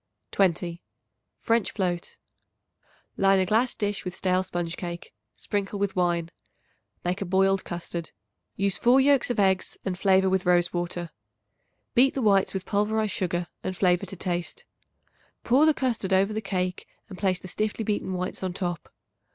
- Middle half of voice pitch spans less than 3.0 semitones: Yes, narrow, 2.6 semitones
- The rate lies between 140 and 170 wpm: Yes, average, 160 wpm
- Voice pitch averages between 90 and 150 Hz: No, high, 190 Hz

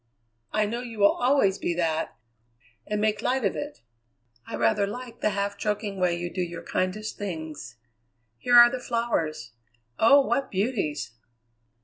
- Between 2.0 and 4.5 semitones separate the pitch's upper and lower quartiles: No, average, 5.2 semitones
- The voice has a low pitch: No, high, 205 Hz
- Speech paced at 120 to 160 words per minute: Yes, average, 155 wpm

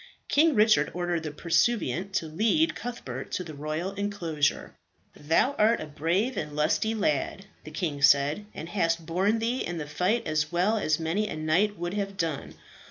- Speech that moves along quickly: No, average, 180 wpm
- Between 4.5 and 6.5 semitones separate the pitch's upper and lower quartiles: Yes, average, 5.2 semitones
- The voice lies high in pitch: No, medium, 175 Hz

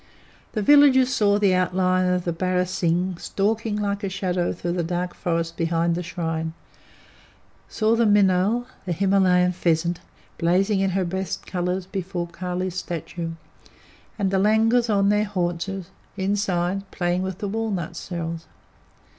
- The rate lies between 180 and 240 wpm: No, average, 140 wpm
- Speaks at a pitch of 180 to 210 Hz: Yes, medium, 185 Hz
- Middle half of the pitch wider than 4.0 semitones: No, narrow, 2.5 semitones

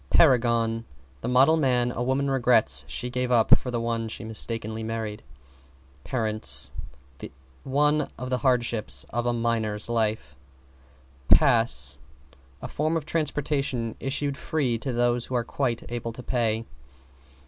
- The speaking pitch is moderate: No, low, 120 Hz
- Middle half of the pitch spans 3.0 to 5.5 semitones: No, narrow, 2.6 semitones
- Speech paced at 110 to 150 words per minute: Yes, slow, 135 wpm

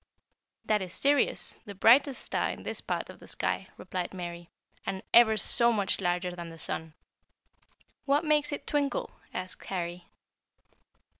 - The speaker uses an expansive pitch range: Yes, wide, 7.2 semitones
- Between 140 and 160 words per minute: Yes, average, 150 wpm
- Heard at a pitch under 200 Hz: Yes, high, 190 Hz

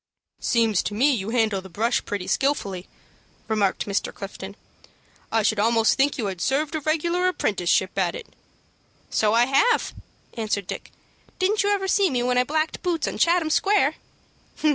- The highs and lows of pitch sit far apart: Yes, wide, 7.3 semitones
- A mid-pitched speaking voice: No, high, 240 Hz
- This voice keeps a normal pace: Yes, average, 165 wpm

